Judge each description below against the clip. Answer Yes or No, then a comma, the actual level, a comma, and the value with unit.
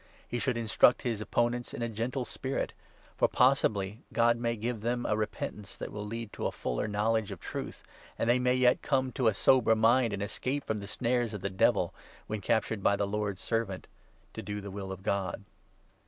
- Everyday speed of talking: No, fast, 215 wpm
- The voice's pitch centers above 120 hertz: No, low, 110 Hz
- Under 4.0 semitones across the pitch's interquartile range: Yes, average, 2.9 semitones